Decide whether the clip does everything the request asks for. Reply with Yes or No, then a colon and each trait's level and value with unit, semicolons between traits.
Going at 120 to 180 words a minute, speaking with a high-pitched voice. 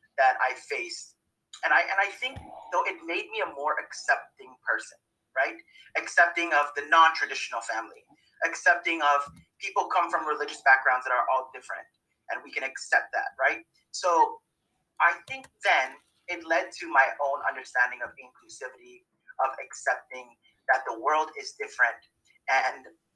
Yes: average, 160 wpm; high, 195 Hz